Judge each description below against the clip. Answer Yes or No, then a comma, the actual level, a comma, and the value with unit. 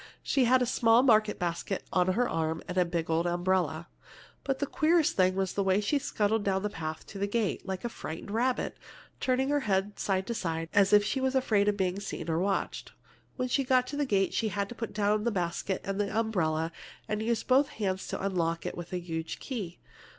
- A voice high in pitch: Yes, high, 200 Hz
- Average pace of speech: No, fast, 225 wpm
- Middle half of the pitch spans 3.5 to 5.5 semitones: Yes, average, 4.6 semitones